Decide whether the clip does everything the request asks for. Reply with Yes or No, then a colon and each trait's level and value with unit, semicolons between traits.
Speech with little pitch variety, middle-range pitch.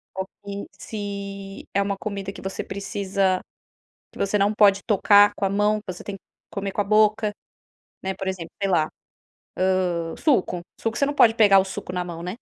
No: narrow, 1.5 semitones; high, 200 Hz